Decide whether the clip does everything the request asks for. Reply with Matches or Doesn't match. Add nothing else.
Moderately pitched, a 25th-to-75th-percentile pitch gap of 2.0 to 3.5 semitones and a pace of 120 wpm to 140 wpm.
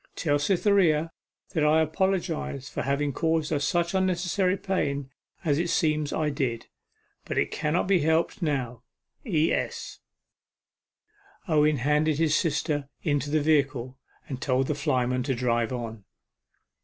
Matches